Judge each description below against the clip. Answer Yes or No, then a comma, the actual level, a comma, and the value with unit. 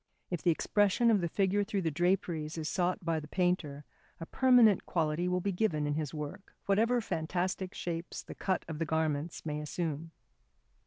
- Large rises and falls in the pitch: No, average, 3.7 semitones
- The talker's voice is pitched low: No, medium, 175 Hz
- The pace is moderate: Yes, average, 180 wpm